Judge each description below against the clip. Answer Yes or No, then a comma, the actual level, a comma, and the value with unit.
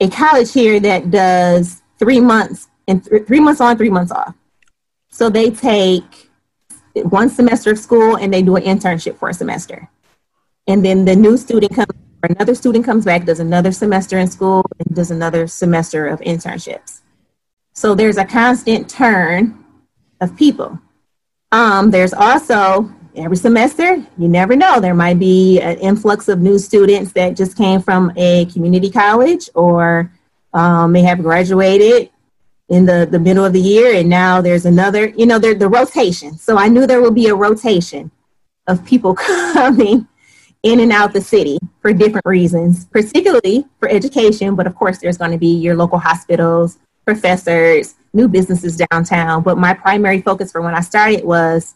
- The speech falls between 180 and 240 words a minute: No, average, 170 wpm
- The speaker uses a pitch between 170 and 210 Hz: Yes, high, 190 Hz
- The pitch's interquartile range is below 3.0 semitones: No, average, 4.0 semitones